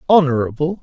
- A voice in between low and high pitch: Yes, medium, 150 Hz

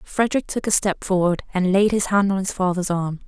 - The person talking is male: No, female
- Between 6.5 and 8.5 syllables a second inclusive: No, 5.6 syllables/s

